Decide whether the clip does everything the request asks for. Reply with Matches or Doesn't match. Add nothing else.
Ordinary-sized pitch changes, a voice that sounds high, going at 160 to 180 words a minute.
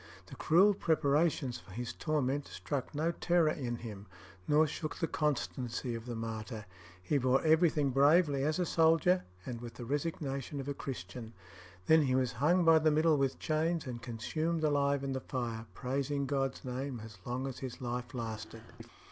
Doesn't match